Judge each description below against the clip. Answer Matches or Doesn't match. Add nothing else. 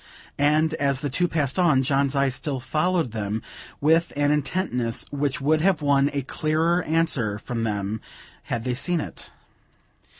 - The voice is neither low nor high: Matches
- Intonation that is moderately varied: Matches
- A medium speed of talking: Matches